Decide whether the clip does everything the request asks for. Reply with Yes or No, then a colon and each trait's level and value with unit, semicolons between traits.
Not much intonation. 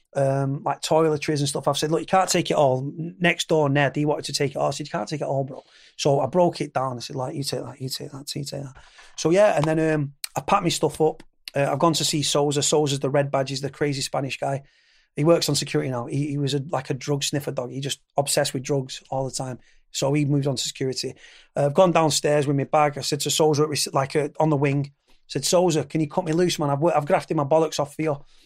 Yes: narrow, 2.1 semitones